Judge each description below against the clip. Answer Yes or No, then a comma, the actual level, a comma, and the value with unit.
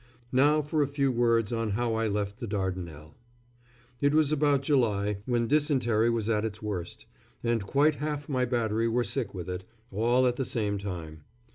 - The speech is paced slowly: No, average, 180 wpm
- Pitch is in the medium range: No, low, 115 Hz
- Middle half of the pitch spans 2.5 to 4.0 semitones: No, average, 4.7 semitones